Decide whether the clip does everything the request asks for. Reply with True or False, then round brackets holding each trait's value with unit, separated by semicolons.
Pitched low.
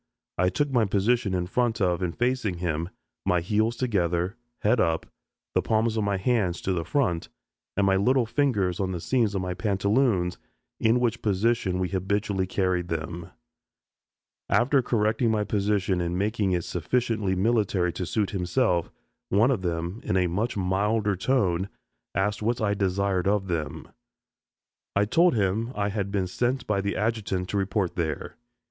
True (100 Hz)